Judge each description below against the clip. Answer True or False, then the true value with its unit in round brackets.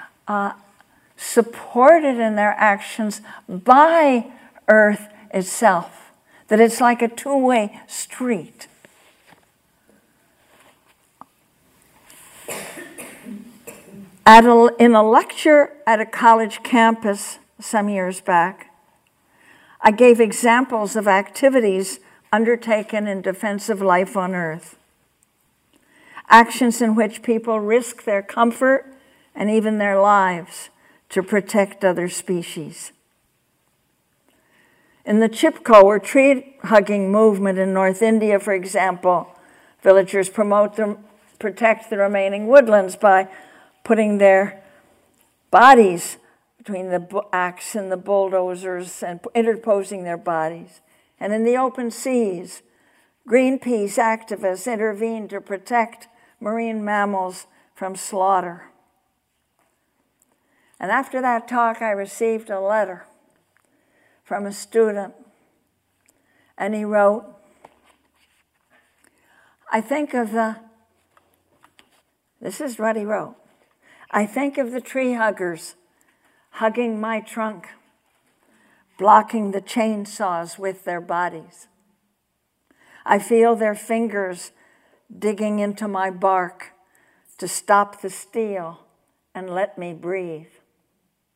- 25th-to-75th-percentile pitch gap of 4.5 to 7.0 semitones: False (3.2 semitones)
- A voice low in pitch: False (210 Hz)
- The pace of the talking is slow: True (100 wpm)